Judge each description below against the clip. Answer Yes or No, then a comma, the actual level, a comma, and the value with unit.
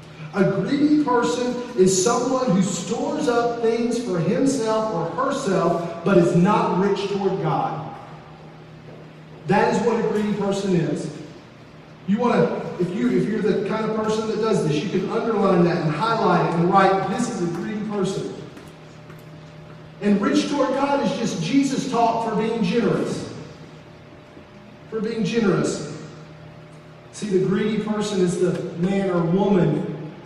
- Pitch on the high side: Yes, high, 200 Hz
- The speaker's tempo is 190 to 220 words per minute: No, average, 155 wpm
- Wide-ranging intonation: No, average, 4.1 semitones